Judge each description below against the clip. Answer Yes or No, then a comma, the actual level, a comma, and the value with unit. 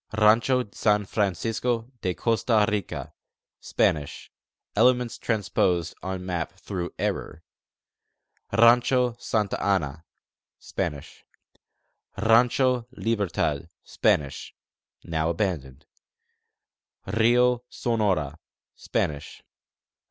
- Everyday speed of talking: No, slow, 75 wpm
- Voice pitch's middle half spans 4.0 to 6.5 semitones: Yes, wide, 5.4 semitones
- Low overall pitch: Yes, low, 105 Hz